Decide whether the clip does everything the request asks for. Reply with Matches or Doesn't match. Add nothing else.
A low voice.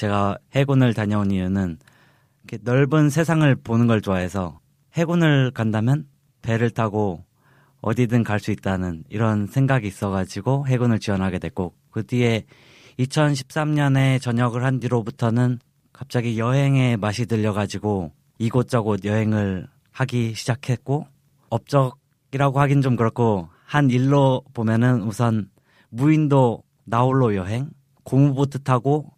Matches